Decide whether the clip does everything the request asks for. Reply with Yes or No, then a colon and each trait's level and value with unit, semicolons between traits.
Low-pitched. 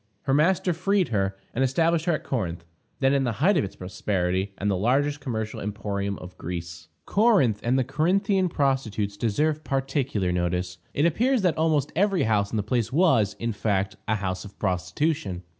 Yes: low, 120 Hz